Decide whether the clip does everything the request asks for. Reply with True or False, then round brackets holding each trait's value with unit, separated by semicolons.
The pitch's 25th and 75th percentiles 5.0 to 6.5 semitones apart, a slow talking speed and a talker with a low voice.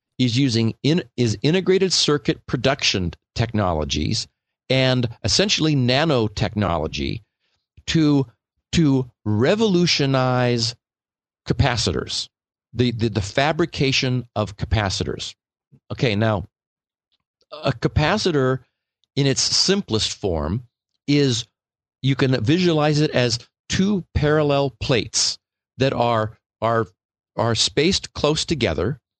True (5.3 semitones; 90 wpm; 125 Hz)